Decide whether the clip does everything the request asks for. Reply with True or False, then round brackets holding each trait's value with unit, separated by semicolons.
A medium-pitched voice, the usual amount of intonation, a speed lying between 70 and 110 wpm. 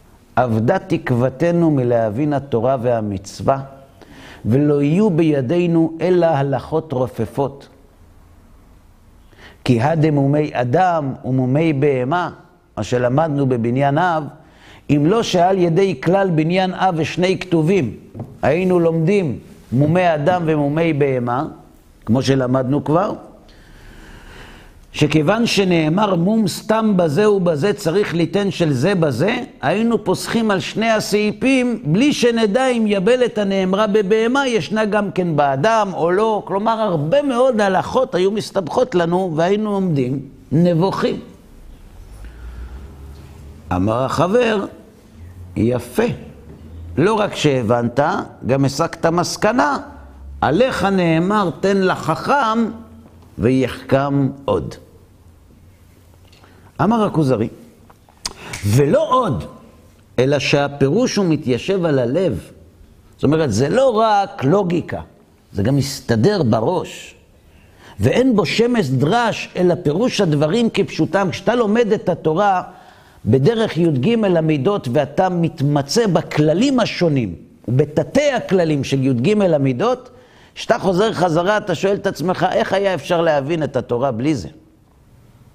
False (155 Hz; 8.1 semitones; 105 wpm)